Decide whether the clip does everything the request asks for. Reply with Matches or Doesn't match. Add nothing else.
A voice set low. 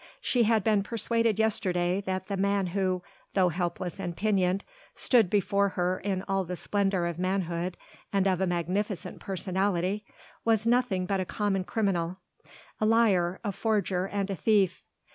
Doesn't match